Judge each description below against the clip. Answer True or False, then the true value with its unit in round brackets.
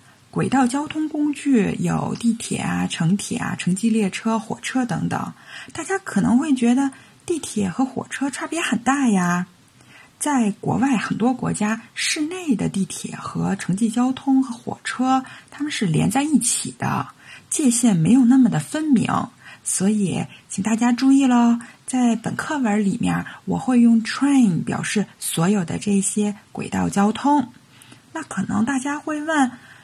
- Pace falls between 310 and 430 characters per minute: False (230 characters per minute)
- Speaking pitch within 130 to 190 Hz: False (235 Hz)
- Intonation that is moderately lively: True (4.6 semitones)